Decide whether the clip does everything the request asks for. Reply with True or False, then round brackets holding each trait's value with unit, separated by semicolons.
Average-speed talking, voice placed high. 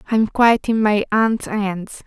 True (175 wpm; 215 Hz)